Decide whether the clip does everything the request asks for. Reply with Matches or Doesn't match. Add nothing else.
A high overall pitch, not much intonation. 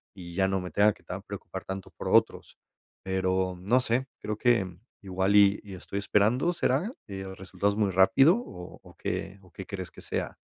Doesn't match